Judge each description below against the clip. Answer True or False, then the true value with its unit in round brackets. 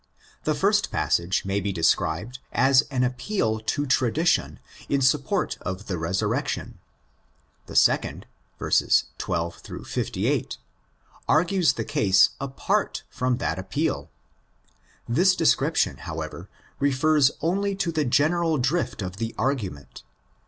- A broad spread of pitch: True (7.9 semitones)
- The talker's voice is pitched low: True (130 Hz)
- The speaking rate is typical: False (115 wpm)